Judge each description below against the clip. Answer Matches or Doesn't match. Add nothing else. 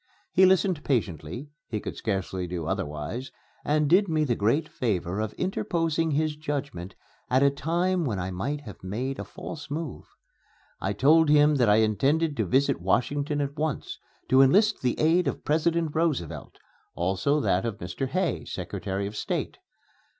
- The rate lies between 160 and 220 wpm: Matches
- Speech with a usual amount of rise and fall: Doesn't match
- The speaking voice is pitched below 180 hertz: Matches